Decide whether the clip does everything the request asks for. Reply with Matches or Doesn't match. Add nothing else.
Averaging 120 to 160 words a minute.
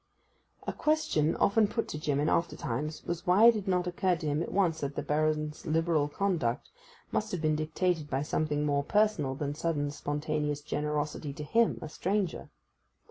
Doesn't match